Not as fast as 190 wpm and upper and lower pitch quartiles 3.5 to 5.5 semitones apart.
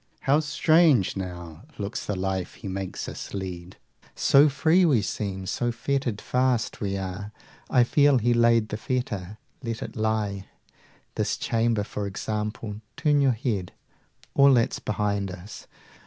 Yes: average, 150 wpm; average, 4.6 semitones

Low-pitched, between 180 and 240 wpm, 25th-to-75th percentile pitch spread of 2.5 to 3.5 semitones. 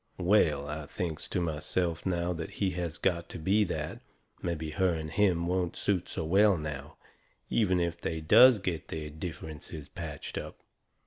No: very low, 85 Hz; average, 170 wpm; average, 2.8 semitones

